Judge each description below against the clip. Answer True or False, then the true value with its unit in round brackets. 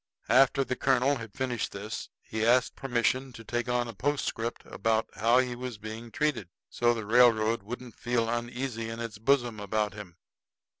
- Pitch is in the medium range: False (120 Hz)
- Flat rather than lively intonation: True (2.2 semitones)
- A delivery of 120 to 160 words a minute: False (170 wpm)